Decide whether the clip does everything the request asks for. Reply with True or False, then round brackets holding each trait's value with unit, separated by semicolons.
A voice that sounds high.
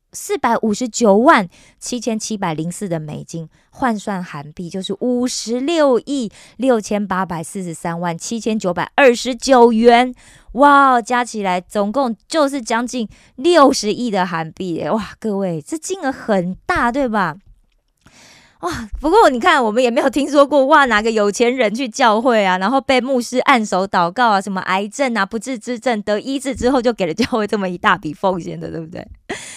True (225 Hz)